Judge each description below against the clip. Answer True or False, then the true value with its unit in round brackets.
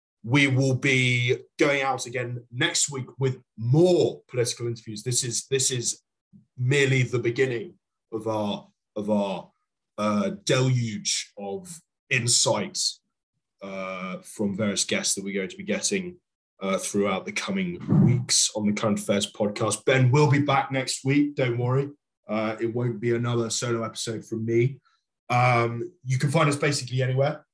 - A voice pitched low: True (125 Hz)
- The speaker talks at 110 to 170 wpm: True (155 wpm)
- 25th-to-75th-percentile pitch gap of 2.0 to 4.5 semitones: True (3.1 semitones)